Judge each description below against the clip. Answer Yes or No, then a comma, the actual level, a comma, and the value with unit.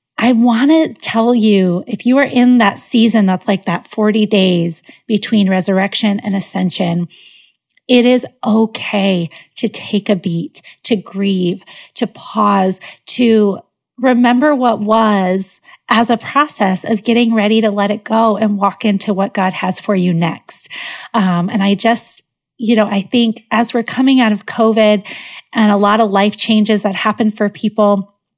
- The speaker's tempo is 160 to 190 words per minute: Yes, average, 165 wpm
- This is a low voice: No, high, 210 Hz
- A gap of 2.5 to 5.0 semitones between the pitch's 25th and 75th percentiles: Yes, average, 2.9 semitones